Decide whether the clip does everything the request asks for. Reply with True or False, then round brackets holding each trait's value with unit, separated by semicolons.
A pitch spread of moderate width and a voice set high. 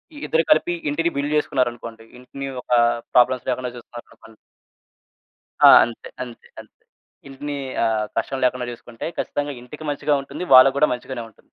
False (3.2 semitones; 130 Hz)